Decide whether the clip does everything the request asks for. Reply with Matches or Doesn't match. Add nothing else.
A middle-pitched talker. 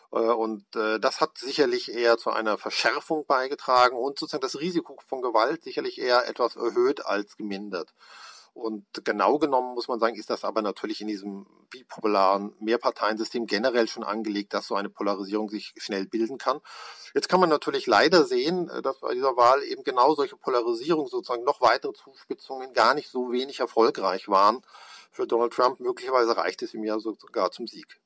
Doesn't match